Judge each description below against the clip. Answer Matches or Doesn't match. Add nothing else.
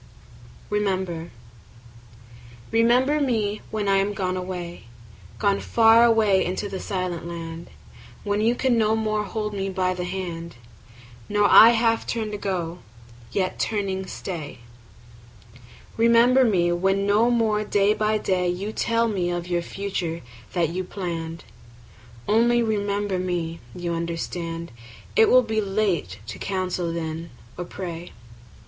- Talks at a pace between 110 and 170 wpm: Matches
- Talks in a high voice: Matches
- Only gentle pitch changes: Doesn't match